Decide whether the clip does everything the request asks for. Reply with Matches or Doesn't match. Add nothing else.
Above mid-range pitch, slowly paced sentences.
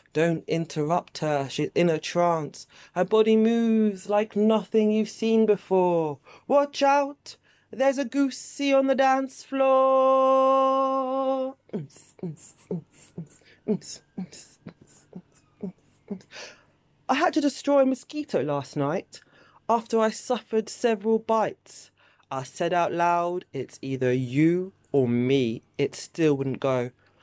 Matches